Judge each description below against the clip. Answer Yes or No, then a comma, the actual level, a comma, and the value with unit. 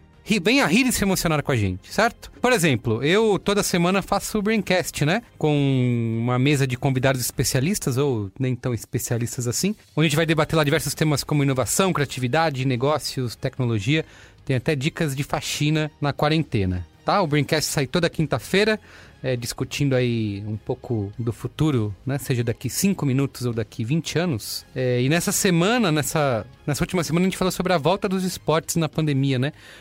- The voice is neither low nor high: Yes, medium, 145 Hz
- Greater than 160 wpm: Yes, average, 185 wpm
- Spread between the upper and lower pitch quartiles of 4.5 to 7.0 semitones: Yes, average, 5.3 semitones